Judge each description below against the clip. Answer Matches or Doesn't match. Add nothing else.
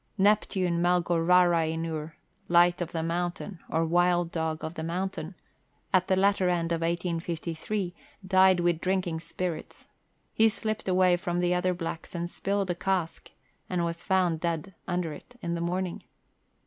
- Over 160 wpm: Doesn't match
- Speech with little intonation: Matches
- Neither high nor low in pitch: Matches